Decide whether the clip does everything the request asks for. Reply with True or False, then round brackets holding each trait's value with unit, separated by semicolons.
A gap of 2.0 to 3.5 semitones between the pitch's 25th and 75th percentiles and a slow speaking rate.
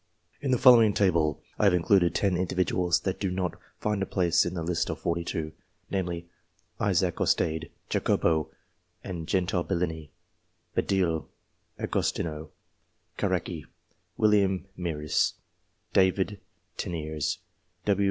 True (3.0 semitones; 125 wpm)